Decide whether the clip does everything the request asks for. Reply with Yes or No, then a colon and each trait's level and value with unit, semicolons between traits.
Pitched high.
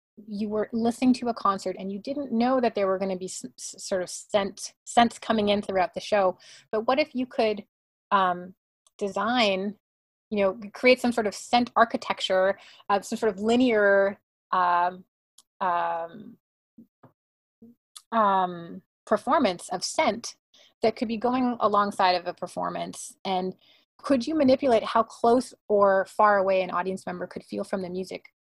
Yes: high, 205 Hz